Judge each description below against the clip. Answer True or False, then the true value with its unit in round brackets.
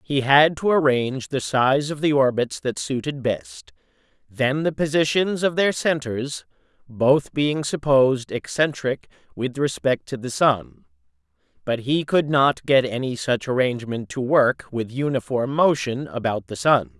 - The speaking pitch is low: True (130 Hz)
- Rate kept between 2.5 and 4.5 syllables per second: True (4.3 syllables/s)